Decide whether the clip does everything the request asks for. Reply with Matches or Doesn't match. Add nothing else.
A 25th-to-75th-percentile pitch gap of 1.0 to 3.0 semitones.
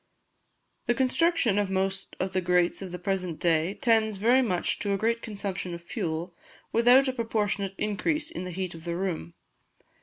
Doesn't match